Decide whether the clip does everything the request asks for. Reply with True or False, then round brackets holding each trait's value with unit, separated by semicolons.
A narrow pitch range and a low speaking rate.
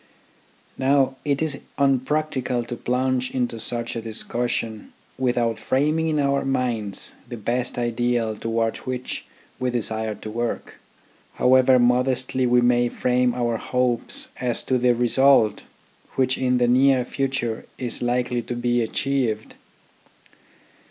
True (1.7 semitones; 130 wpm)